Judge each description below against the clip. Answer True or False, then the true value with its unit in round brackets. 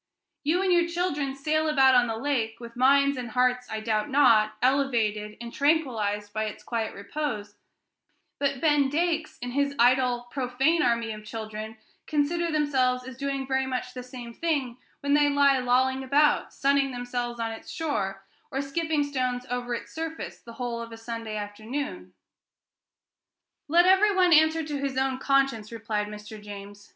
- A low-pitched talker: False (255 Hz)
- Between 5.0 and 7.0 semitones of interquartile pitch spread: False (3.8 semitones)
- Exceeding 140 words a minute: True (165 wpm)